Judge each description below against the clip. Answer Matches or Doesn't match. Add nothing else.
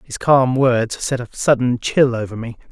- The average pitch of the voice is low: Matches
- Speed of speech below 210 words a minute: Matches